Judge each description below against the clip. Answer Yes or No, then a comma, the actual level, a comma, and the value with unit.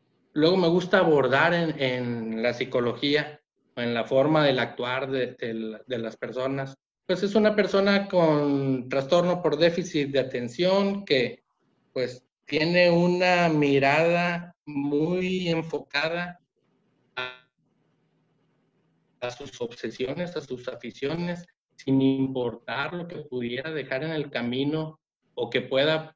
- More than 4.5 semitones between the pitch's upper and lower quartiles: Yes, average, 5.2 semitones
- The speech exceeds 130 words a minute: No, slow, 125 wpm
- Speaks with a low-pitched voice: No, medium, 145 Hz